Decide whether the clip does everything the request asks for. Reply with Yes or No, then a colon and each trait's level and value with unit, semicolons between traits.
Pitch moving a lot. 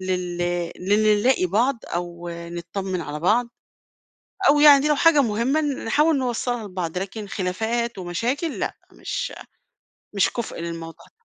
Yes: wide, 6.3 semitones